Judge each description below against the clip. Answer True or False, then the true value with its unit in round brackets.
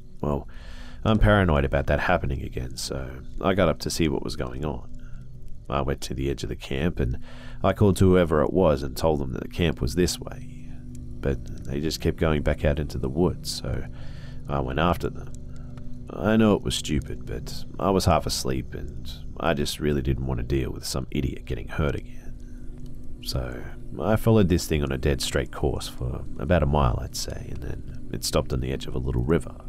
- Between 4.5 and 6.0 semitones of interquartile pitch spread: True (4.9 semitones)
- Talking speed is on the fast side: True (215 wpm)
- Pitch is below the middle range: True (70 Hz)